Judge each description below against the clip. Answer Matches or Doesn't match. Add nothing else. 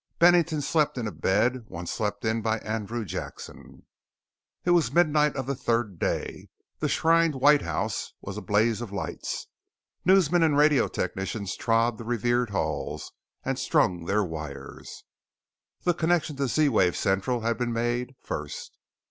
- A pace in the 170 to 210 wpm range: Doesn't match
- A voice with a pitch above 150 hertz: Doesn't match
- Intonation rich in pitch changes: Matches